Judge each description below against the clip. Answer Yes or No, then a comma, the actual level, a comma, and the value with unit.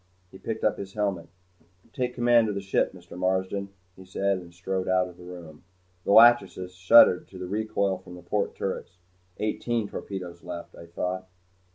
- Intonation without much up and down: Yes, narrow, 2.3 semitones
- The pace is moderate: Yes, average, 180 wpm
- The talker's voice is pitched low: Yes, very low, 95 Hz